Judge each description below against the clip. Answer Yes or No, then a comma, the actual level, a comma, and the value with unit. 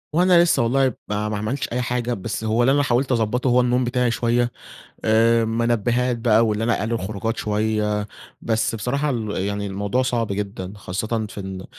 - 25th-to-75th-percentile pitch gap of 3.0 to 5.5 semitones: No, narrow, 2.6 semitones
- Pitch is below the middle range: Yes, low, 115 Hz